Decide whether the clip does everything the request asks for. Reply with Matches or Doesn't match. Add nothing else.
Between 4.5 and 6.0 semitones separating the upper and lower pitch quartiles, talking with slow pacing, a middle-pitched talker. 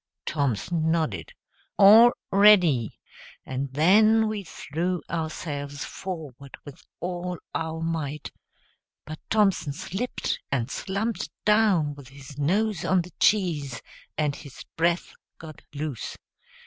Matches